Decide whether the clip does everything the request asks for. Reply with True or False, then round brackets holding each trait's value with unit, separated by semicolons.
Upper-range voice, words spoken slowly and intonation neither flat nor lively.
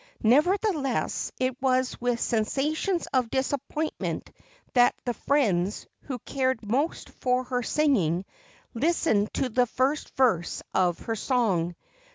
True (255 Hz; 120 wpm; 3.9 semitones)